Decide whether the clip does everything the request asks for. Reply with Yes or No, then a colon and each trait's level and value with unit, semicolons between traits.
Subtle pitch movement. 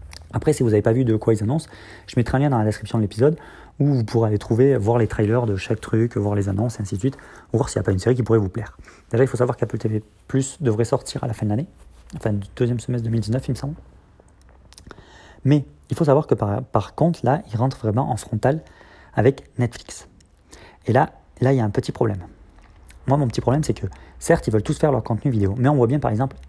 No: average, 3.9 semitones